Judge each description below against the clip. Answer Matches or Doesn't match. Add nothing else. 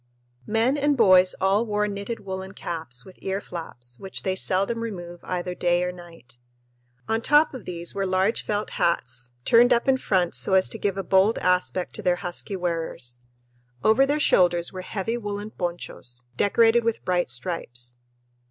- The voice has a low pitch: Doesn't match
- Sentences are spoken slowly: Doesn't match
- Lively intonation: Doesn't match